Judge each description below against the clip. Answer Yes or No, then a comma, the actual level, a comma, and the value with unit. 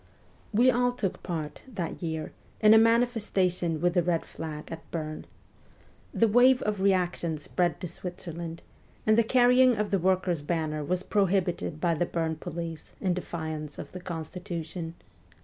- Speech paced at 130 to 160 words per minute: Yes, average, 155 wpm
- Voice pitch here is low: No, medium, 175 Hz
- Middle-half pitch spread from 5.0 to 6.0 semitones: No, average, 4.2 semitones